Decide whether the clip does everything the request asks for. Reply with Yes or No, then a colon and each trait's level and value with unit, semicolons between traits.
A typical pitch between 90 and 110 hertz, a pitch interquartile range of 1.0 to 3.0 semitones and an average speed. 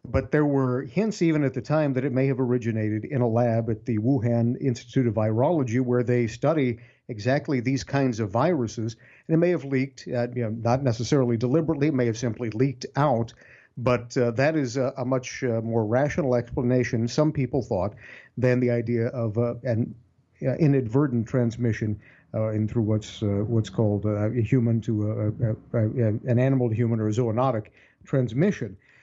No: low, 125 Hz; narrow, 2.6 semitones; average, 185 wpm